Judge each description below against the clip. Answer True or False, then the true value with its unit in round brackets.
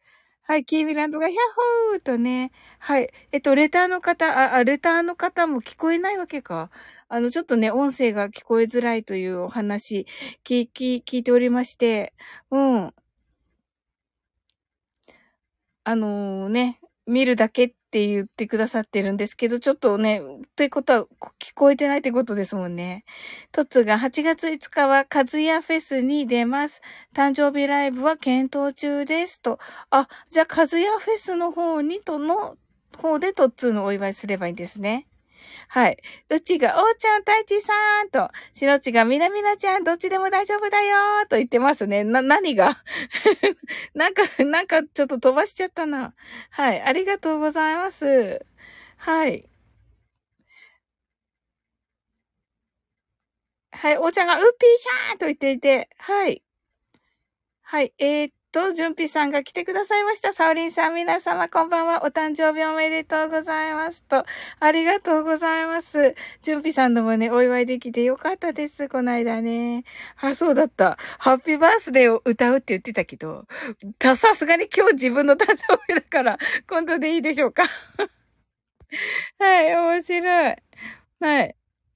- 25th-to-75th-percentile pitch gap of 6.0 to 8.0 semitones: False (5.4 semitones)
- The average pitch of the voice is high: True (290 Hz)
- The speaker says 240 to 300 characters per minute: False (315 characters per minute)